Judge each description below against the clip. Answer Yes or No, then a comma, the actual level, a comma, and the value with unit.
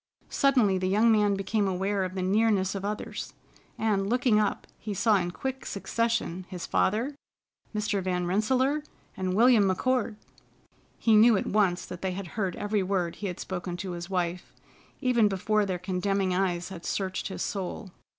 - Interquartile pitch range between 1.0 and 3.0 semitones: Yes, average, 2.7 semitones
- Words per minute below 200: Yes, average, 170 wpm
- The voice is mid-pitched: No, high, 195 Hz